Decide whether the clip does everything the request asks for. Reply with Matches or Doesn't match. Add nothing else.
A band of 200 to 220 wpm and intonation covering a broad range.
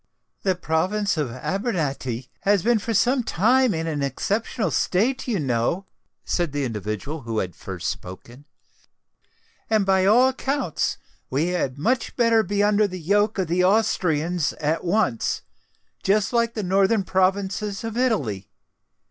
Doesn't match